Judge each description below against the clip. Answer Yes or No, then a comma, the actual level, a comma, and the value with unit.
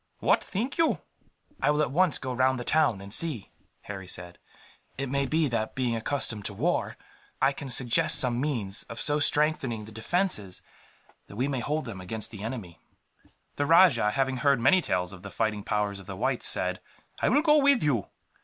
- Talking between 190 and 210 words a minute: Yes, average, 195 wpm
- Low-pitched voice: Yes, low, 125 Hz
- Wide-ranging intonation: Yes, wide, 6.0 semitones